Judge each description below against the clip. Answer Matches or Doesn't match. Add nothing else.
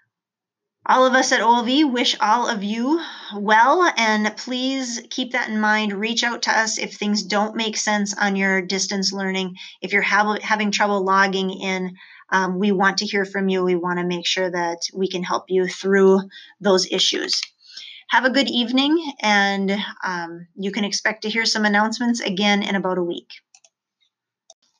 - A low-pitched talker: Doesn't match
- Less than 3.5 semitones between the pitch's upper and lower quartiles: Matches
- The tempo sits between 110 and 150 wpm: Doesn't match